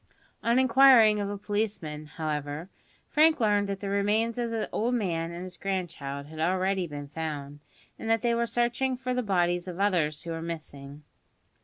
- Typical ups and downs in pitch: No, wide, 5.9 semitones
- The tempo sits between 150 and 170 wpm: No, average, 180 wpm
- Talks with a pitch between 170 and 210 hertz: Yes, high, 190 Hz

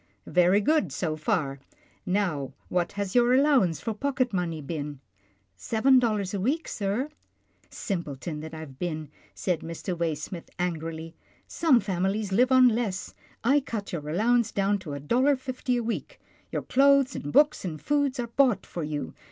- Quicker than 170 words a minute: Yes, average, 195 wpm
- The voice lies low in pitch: No, high, 195 Hz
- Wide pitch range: Yes, wide, 7.4 semitones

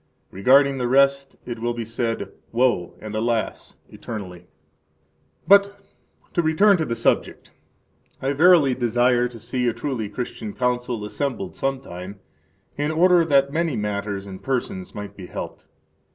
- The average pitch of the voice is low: Yes, low, 125 Hz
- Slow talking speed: No, average, 150 wpm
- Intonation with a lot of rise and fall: No, average, 4.6 semitones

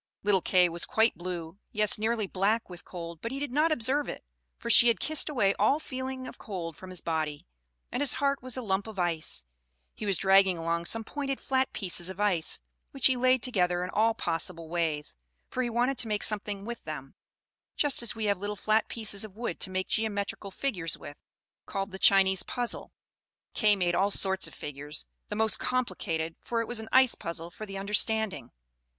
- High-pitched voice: Yes, high, 205 Hz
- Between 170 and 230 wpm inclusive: Yes, fast, 205 wpm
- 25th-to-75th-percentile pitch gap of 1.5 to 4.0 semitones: No, average, 4.9 semitones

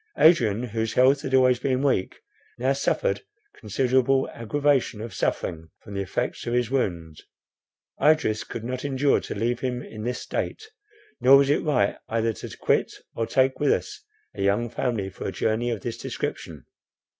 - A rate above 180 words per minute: No, average, 170 wpm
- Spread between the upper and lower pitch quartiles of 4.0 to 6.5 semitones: No, average, 3.3 semitones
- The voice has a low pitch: Yes, low, 120 Hz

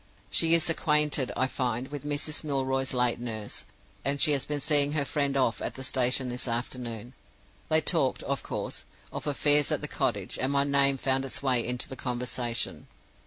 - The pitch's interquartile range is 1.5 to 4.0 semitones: Yes, average, 2.7 semitones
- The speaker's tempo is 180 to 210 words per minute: Yes, average, 185 wpm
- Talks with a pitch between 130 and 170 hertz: Yes, low, 135 Hz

